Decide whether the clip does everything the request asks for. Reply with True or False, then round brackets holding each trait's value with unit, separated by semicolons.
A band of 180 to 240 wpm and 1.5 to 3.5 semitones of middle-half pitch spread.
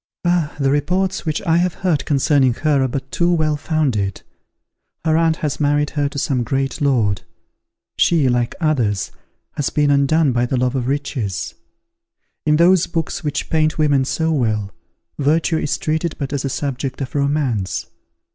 False (165 wpm; 3.1 semitones)